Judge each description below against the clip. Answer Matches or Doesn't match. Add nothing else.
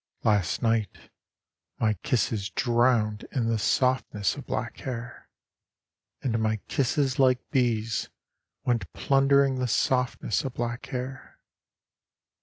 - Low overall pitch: Matches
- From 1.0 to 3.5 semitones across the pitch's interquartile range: Matches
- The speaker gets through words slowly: Matches